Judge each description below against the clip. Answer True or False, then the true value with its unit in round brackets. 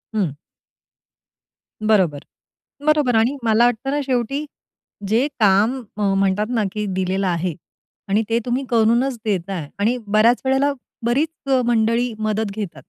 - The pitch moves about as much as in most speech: True (3.7 semitones)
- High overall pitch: True (220 Hz)